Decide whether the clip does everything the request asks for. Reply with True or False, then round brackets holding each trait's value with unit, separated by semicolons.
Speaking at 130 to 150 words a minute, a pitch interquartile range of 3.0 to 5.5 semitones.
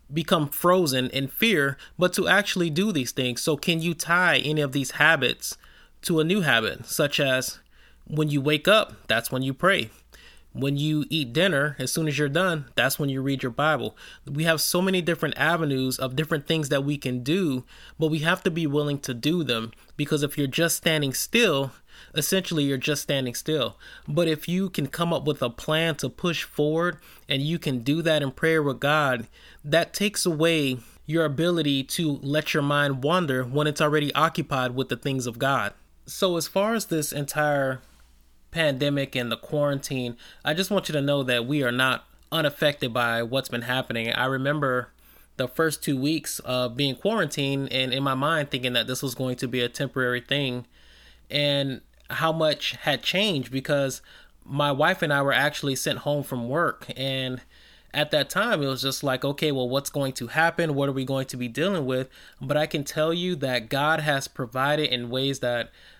False (200 wpm; 3.4 semitones)